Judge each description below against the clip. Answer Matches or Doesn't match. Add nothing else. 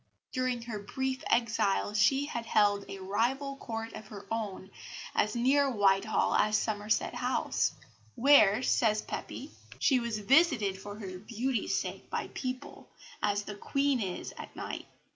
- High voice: Matches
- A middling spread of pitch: Matches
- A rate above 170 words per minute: Doesn't match